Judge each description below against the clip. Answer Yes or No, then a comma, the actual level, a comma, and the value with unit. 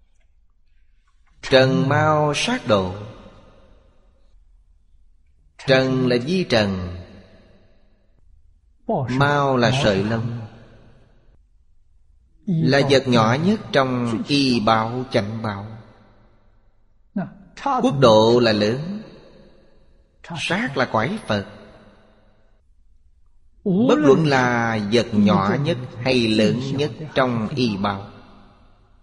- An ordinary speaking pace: No, slow, 85 wpm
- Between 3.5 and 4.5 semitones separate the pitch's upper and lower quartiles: No, wide, 5.4 semitones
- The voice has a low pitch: Yes, low, 110 Hz